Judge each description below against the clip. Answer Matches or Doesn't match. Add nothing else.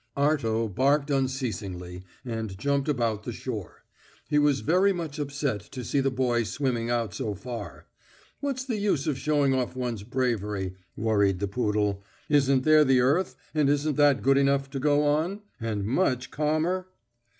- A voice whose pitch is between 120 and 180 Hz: Matches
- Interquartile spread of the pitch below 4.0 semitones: Doesn't match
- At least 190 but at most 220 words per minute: Doesn't match